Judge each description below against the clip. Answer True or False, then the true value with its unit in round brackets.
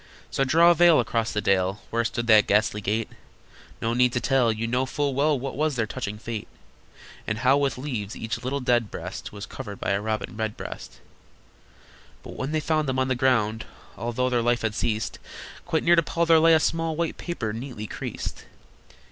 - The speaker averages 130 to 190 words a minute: False (200 wpm)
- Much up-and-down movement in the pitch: False (4.6 semitones)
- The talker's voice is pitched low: True (120 Hz)